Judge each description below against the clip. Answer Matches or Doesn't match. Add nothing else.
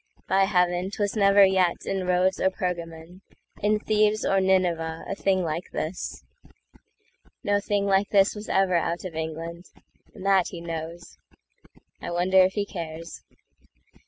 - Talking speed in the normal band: Doesn't match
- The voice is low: Doesn't match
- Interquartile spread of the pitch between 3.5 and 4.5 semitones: Doesn't match